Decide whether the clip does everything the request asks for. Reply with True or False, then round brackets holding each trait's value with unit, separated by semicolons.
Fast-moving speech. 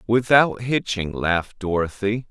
False (105 wpm)